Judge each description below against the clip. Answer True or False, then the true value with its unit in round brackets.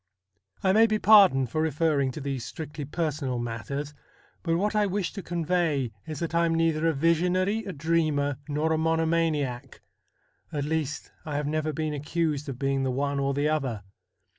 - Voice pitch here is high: False (155 Hz)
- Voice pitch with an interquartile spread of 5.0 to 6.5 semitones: False (3.1 semitones)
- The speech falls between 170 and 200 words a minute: True (180 wpm)